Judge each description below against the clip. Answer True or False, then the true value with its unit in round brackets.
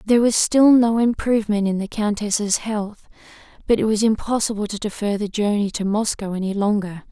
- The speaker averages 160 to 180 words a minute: True (175 wpm)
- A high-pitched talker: True (210 Hz)